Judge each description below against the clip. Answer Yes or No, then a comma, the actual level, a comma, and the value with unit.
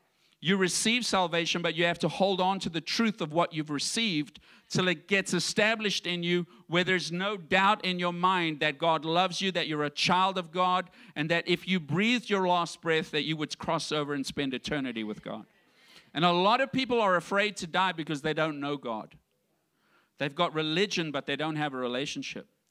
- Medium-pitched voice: Yes, medium, 175 Hz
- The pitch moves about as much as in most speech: Yes, average, 3.4 semitones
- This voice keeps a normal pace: No, fast, 210 wpm